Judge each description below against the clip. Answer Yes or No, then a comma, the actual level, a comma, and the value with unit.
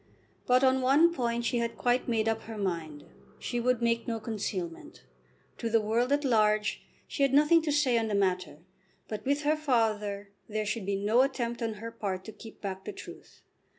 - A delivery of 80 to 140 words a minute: No, average, 200 wpm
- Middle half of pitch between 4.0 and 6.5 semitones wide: No, average, 3.3 semitones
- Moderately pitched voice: No, high, 230 Hz